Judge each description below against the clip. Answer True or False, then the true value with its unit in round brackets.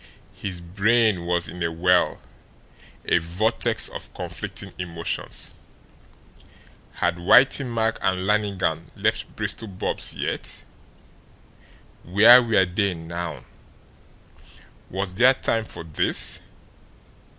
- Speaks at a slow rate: True (100 wpm)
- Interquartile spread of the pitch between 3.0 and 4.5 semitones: True (4.1 semitones)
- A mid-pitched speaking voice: False (95 Hz)